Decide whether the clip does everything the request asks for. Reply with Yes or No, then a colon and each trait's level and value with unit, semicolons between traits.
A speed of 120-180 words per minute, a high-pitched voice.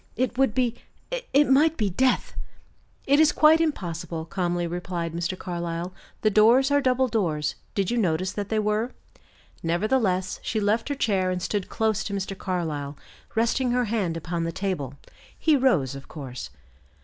Yes: average, 165 wpm; high, 200 Hz